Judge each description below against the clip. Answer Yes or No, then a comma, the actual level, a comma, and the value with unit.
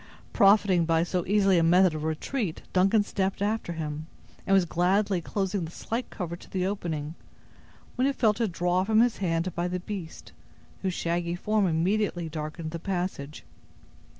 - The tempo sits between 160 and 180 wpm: Yes, average, 170 wpm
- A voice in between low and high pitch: Yes, medium, 180 Hz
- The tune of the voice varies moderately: Yes, average, 3.3 semitones